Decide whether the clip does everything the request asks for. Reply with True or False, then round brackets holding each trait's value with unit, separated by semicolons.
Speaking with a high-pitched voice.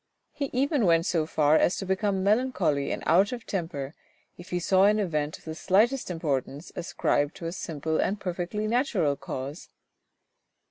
False (175 Hz)